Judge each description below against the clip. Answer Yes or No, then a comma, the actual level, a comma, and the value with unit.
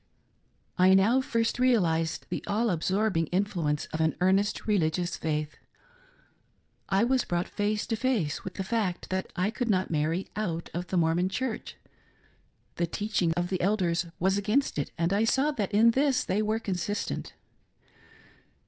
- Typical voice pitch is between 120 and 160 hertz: No, high, 190 Hz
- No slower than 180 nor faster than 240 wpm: No, average, 155 wpm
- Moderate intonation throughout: Yes, average, 4.1 semitones